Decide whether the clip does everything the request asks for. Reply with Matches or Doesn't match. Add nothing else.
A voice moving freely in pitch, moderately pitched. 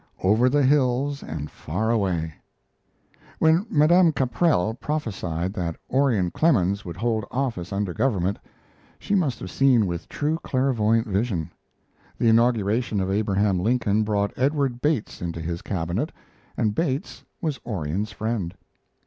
Doesn't match